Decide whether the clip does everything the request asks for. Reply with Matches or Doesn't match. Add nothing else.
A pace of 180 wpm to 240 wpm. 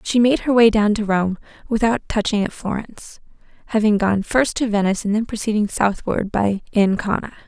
Doesn't match